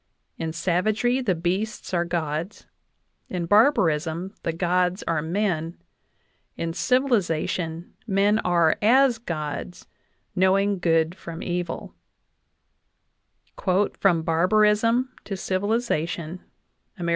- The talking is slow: Yes, slow, 95 wpm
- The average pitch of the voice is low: No, medium, 180 Hz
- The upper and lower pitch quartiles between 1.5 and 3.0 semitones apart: No, average, 4.0 semitones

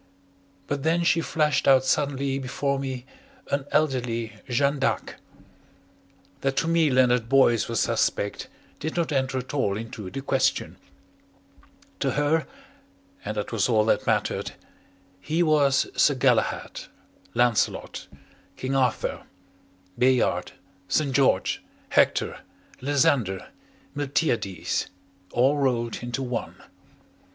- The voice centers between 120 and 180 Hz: Yes, low, 135 Hz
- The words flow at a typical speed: No, slow, 115 wpm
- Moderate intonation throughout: Yes, average, 3.0 semitones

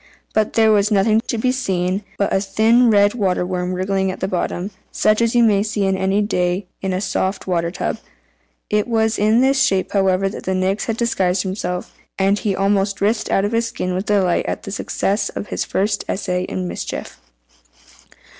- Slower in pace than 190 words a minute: No, average, 195 wpm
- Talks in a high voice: Yes, high, 195 Hz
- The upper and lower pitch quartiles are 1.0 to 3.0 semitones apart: Yes, narrow, 2.4 semitones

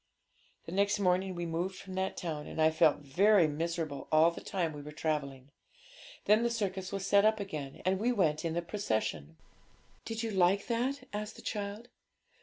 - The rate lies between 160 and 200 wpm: Yes, average, 190 wpm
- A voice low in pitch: No, medium, 185 Hz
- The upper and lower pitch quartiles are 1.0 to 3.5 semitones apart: No, average, 4.5 semitones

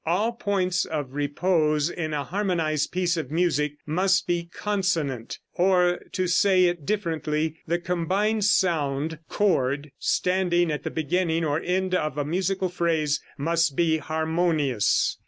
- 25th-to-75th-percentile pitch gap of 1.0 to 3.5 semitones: Yes, average, 3.2 semitones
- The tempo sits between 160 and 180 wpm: No, average, 140 wpm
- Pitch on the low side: No, medium, 170 Hz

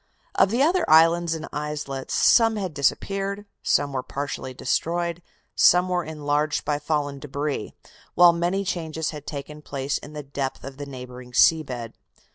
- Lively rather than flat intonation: No, average, 3.7 semitones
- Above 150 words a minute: Yes, average, 160 wpm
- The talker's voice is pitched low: No, medium, 150 Hz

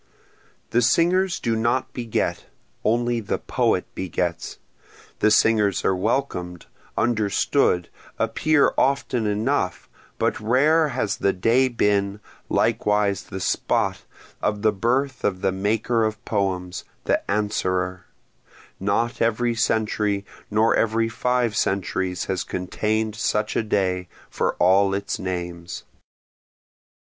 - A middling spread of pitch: Yes, average, 3.6 semitones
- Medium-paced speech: No, slow, 115 wpm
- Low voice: Yes, low, 105 Hz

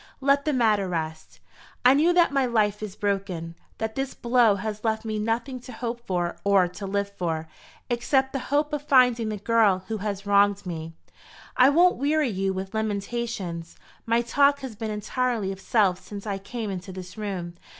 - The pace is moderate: Yes, average, 185 wpm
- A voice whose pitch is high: Yes, high, 215 Hz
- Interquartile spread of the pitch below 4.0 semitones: No, average, 4.3 semitones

